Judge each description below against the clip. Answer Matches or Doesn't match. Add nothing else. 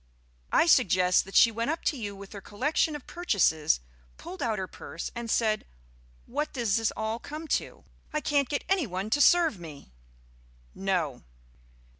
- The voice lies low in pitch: Doesn't match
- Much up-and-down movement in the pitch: Matches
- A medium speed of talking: Matches